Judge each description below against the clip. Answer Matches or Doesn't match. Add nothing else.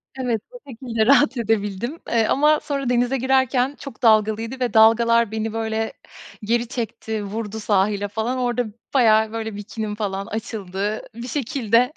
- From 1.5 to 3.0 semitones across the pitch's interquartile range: Matches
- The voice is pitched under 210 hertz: Doesn't match